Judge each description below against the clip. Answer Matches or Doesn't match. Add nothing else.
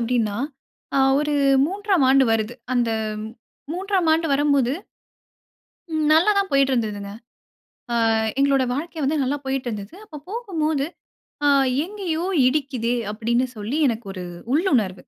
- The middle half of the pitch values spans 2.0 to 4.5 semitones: Doesn't match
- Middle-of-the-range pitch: Doesn't match